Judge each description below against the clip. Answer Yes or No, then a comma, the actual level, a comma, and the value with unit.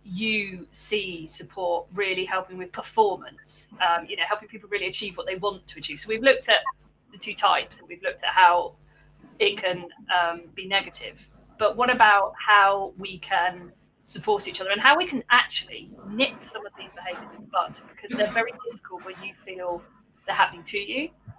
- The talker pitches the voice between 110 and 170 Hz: No, high, 205 Hz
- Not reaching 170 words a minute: No, average, 195 wpm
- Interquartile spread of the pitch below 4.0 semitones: No, average, 4.8 semitones